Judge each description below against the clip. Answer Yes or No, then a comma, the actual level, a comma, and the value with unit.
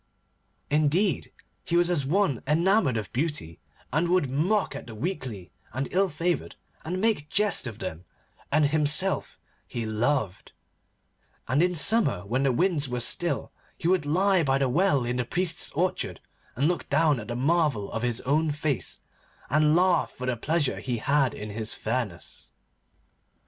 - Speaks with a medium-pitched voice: Yes, medium, 145 Hz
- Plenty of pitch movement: Yes, wide, 5.9 semitones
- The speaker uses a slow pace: No, average, 165 wpm